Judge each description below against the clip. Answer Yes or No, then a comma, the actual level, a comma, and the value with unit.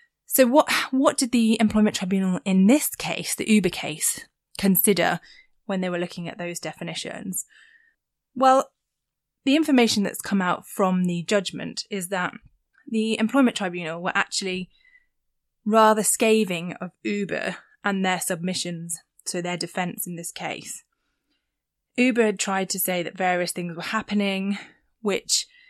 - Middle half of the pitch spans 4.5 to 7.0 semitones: Yes, average, 5.2 semitones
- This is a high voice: Yes, high, 200 Hz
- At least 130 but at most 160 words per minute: Yes, average, 140 wpm